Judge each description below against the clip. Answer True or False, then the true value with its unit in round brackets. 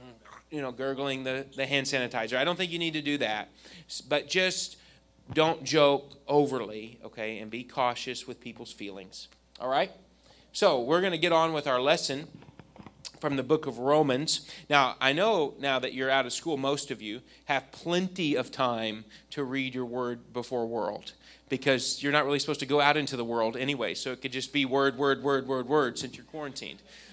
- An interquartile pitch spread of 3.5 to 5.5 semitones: False (2.8 semitones)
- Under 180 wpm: False (200 wpm)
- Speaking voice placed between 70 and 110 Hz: False (135 Hz)